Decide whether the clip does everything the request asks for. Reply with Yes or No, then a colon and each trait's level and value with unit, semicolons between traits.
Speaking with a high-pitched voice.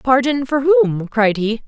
Yes: high, 245 Hz